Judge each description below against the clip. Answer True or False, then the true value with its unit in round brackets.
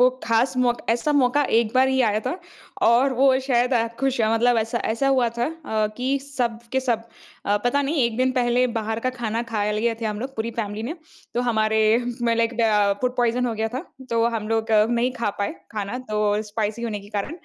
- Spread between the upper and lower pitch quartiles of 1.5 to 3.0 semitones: True (2.6 semitones)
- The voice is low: False (235 Hz)